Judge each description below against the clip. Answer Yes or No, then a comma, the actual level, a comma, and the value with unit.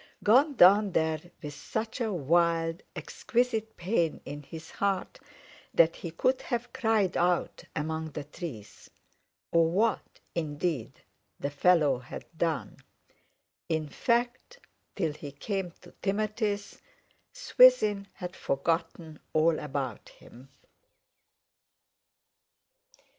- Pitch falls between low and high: Yes, medium, 170 Hz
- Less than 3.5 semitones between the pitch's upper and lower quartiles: No, wide, 5.5 semitones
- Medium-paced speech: No, slow, 105 wpm